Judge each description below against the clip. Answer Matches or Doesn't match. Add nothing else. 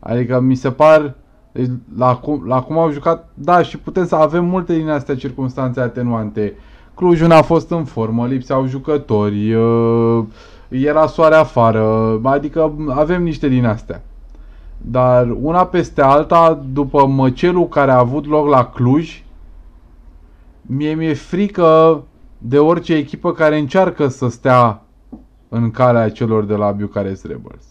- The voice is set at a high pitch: Doesn't match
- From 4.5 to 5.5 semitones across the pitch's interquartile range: Matches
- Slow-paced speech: Doesn't match